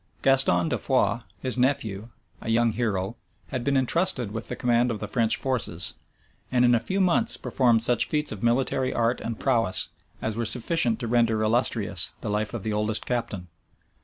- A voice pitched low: Yes, low, 115 Hz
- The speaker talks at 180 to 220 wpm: Yes, average, 185 wpm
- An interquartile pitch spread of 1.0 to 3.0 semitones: Yes, average, 2.7 semitones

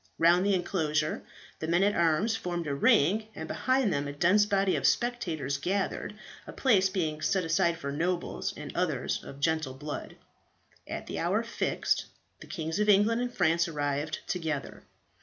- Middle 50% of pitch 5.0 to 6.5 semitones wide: No, average, 4.4 semitones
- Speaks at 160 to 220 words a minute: Yes, average, 170 wpm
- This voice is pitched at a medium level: Yes, medium, 170 Hz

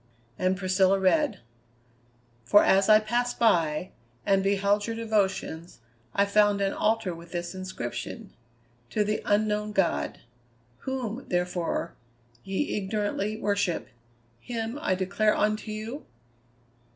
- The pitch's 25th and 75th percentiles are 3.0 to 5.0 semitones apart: No, narrow, 2.4 semitones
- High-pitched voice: Yes, high, 205 Hz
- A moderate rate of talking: No, slow, 115 wpm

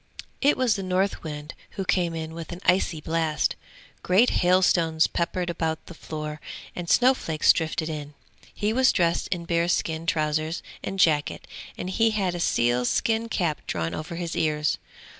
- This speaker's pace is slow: No, average, 160 wpm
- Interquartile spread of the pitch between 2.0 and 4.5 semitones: Yes, average, 2.9 semitones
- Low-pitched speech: No, medium, 170 Hz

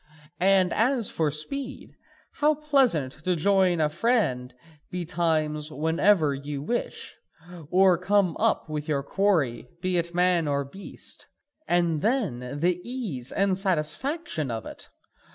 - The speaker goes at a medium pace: No, slow, 130 wpm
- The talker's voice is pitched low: No, medium, 175 Hz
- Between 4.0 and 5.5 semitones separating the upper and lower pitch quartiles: Yes, average, 4.9 semitones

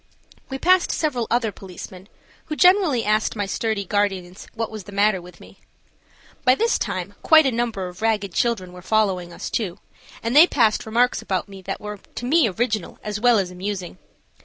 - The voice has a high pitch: Yes, high, 215 Hz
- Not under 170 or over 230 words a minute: Yes, average, 185 wpm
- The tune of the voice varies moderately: Yes, average, 4.1 semitones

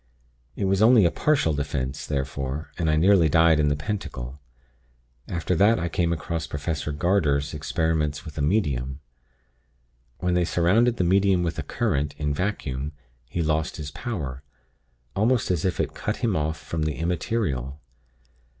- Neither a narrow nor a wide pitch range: Yes, average, 4.4 semitones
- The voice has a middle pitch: No, very low, 80 Hz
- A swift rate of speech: No, average, 160 wpm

